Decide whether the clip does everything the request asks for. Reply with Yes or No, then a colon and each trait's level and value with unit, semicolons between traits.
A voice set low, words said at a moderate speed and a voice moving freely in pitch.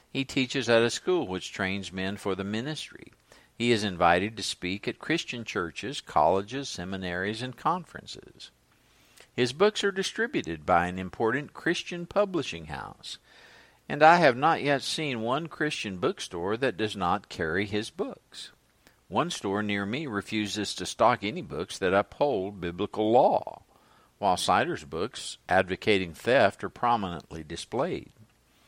Yes: low, 110 Hz; average, 145 wpm; wide, 6.1 semitones